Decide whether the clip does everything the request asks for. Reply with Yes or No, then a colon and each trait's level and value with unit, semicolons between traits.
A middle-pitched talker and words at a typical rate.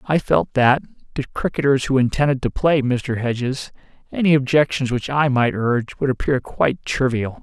No: low, 130 Hz; average, 170 wpm